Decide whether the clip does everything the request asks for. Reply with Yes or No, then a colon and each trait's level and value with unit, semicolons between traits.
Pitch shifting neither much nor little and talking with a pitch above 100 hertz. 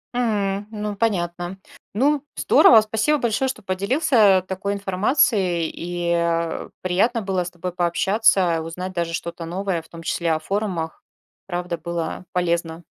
Yes: average, 3.5 semitones; medium, 185 Hz